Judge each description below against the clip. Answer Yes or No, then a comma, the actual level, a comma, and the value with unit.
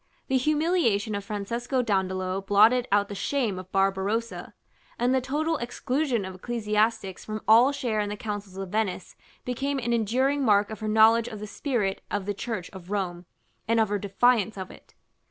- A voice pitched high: Yes, high, 215 Hz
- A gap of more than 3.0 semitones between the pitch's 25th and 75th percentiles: Yes, average, 3.5 semitones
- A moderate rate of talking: Yes, average, 180 wpm